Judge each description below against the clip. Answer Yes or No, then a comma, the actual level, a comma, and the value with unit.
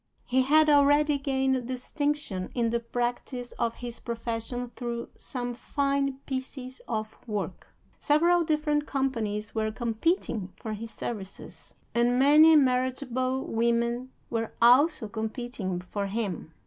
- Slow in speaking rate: Yes, slow, 120 wpm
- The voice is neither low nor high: No, high, 245 Hz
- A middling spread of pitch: Yes, average, 3.4 semitones